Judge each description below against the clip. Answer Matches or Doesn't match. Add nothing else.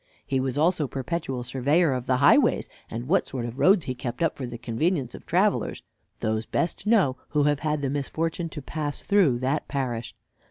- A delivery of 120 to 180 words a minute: Doesn't match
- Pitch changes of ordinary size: Matches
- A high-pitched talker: Doesn't match